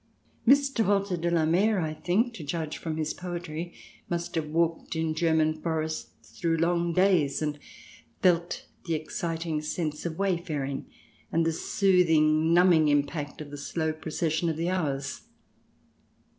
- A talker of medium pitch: Yes, medium, 165 Hz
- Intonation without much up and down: Yes, narrow, 2.0 semitones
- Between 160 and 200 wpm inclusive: No, average, 150 wpm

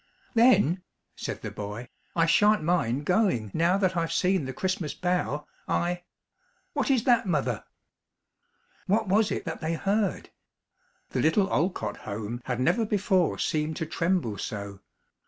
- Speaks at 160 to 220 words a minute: No, average, 145 wpm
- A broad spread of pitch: Yes, wide, 6.6 semitones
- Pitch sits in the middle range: Yes, medium, 170 Hz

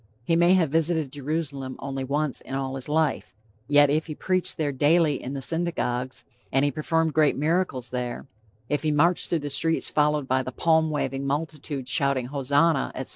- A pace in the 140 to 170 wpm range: No, average, 185 wpm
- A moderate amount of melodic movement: Yes, average, 3.0 semitones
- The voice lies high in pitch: No, medium, 145 Hz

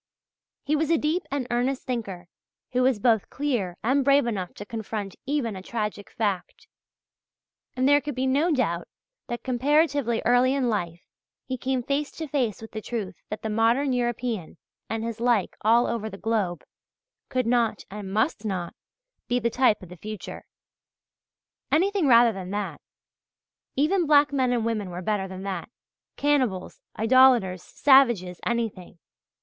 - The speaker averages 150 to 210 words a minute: Yes, average, 160 wpm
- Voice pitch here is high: Yes, high, 235 Hz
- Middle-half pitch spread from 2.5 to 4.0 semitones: No, average, 4.4 semitones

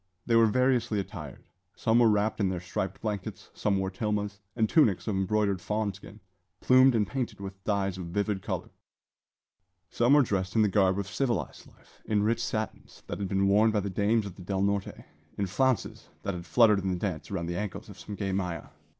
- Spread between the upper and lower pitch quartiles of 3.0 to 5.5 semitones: No, narrow, 2.4 semitones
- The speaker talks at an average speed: No, fast, 210 wpm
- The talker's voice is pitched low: Yes, low, 100 Hz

